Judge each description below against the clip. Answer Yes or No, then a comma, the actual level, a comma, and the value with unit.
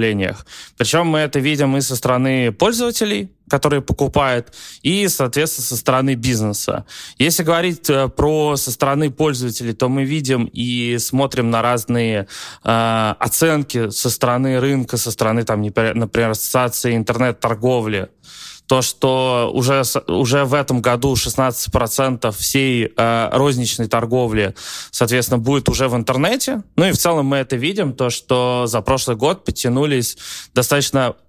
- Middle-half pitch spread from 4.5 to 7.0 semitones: No, average, 2.8 semitones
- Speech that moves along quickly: No, average, 135 wpm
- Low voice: Yes, low, 125 Hz